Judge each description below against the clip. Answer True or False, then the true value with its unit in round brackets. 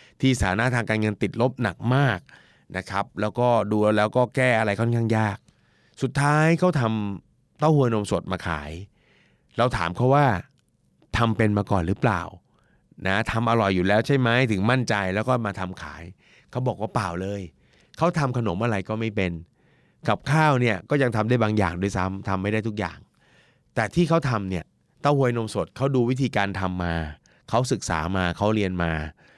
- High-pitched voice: False (110 Hz)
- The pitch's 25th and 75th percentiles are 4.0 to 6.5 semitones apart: True (4.7 semitones)